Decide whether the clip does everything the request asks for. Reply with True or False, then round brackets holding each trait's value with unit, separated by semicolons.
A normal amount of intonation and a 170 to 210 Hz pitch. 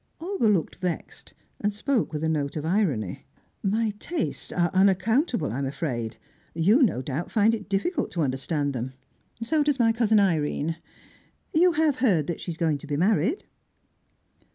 False (7.2 semitones; 185 Hz)